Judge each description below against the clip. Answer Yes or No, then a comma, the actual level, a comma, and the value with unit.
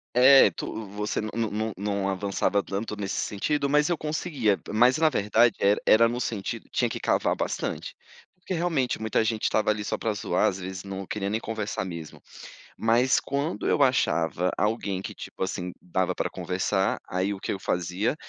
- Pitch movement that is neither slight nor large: Yes, average, 4.0 semitones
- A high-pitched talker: No, low, 105 Hz